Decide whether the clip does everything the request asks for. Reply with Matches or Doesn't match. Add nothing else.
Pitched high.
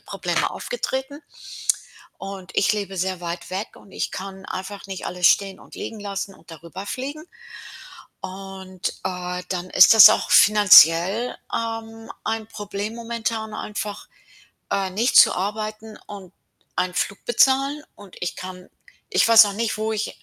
Matches